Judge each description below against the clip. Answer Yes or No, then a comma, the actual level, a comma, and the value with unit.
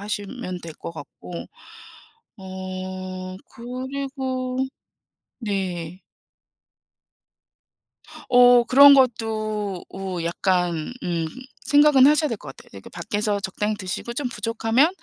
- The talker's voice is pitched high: Yes, high, 210 Hz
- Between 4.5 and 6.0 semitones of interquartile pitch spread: Yes, wide, 5.4 semitones